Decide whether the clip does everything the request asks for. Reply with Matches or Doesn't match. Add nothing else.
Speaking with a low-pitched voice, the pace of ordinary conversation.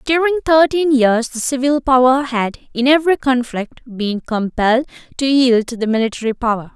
Doesn't match